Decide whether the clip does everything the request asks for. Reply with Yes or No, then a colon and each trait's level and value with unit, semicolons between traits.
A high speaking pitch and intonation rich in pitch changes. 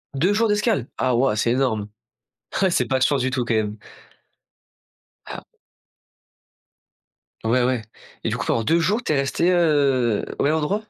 No: low, 135 Hz; wide, 5.7 semitones